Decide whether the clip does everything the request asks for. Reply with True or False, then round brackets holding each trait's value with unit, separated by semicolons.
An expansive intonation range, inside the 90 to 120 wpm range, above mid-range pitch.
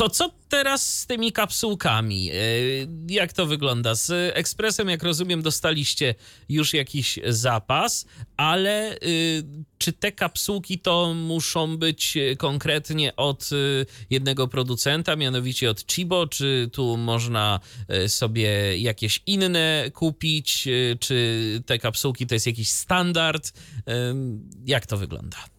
False (6.0 semitones; 115 wpm; 140 Hz)